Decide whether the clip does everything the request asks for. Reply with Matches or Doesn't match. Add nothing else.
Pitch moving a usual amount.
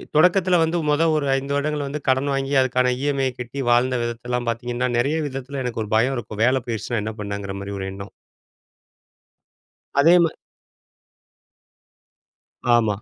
Matches